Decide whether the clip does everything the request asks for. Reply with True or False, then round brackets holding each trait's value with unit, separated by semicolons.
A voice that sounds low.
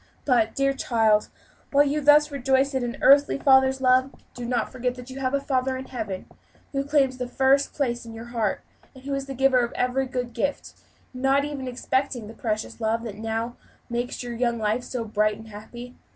False (255 Hz)